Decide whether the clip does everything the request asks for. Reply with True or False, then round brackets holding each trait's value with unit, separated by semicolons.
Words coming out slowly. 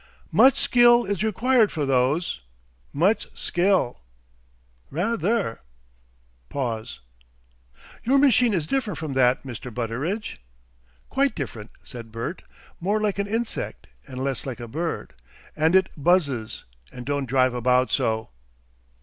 True (125 wpm)